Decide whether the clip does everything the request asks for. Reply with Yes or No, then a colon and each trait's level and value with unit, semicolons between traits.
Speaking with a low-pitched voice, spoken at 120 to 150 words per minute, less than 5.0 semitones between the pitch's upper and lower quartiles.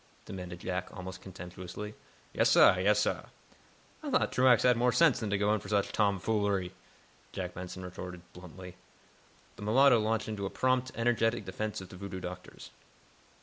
No: low, 100 Hz; average, 165 wpm; average, 3.6 semitones